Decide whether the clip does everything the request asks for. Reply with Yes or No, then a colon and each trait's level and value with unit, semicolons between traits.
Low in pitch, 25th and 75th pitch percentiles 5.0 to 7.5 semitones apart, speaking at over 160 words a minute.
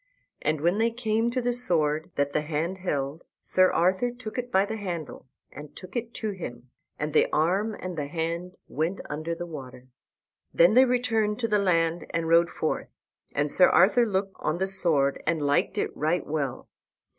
No: medium, 175 Hz; wide, 5.5 semitones; average, 190 wpm